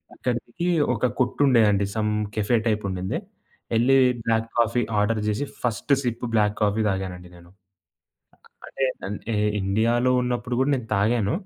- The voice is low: Yes, low, 115 Hz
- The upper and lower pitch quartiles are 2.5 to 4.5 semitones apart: Yes, average, 2.9 semitones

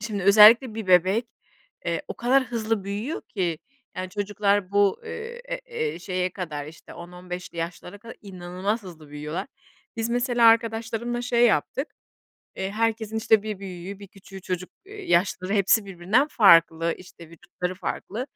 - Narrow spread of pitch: No, average, 4.0 semitones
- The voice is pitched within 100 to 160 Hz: No, high, 200 Hz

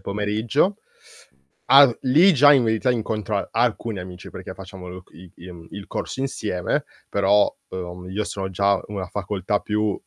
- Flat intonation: No, average, 3.8 semitones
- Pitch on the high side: No, low, 100 Hz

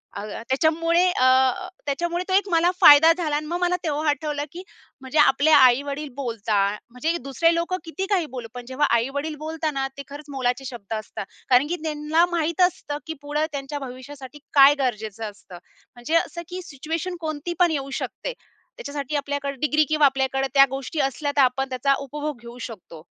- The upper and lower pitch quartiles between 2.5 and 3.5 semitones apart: Yes, average, 3.2 semitones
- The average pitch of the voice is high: Yes, very high, 285 Hz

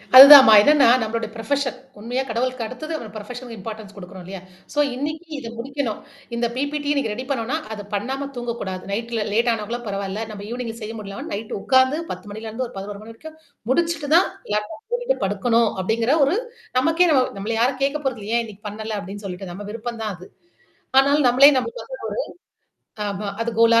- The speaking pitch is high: Yes, high, 230 Hz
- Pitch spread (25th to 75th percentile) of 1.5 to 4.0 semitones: No, average, 4.4 semitones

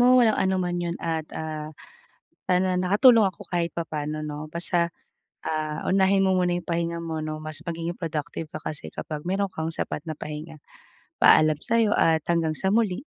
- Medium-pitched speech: Yes, medium, 170 Hz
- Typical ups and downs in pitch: Yes, average, 3.0 semitones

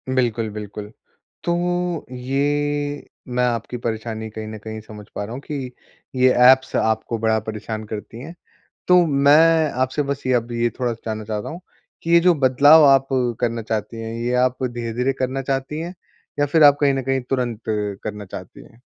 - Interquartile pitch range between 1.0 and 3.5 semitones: No, average, 4.2 semitones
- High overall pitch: No, low, 125 Hz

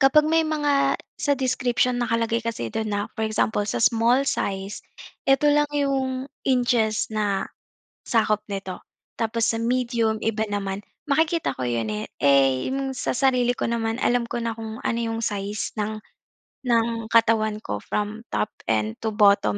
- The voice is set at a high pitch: Yes, high, 225 Hz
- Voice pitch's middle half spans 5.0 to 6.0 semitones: No, average, 3.3 semitones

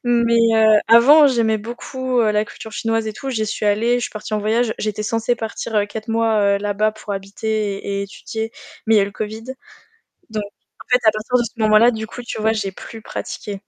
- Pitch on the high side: Yes, high, 220 Hz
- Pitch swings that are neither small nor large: No, narrow, 1.7 semitones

